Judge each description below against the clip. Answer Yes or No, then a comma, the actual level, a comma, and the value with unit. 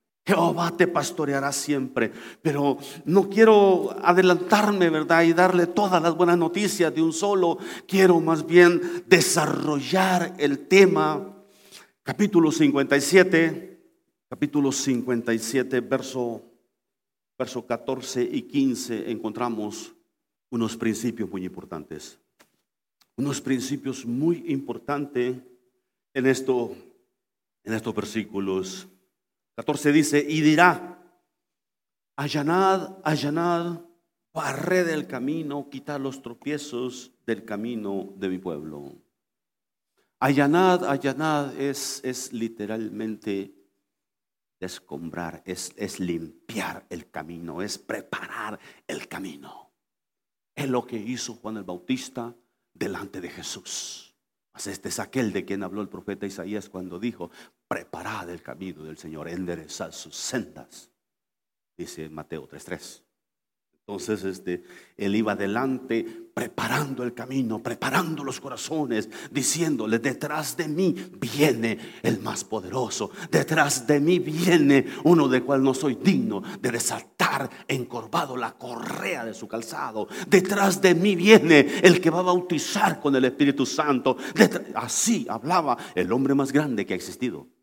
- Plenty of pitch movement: Yes, wide, 7.1 semitones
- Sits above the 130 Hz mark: Yes, medium, 140 Hz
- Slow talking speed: Yes, slow, 115 wpm